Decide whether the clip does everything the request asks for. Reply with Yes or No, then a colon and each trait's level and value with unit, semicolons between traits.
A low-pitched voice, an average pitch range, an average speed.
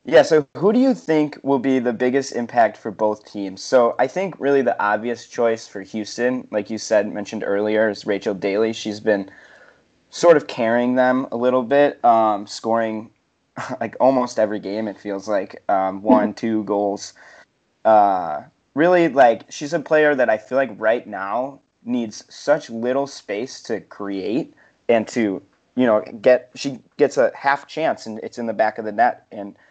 Yes: low, 115 Hz; average, 4.1 semitones; average, 180 wpm